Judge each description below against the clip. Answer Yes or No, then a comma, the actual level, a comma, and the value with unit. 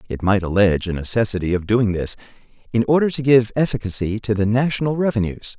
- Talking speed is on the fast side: No, average, 185 wpm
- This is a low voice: Yes, low, 110 Hz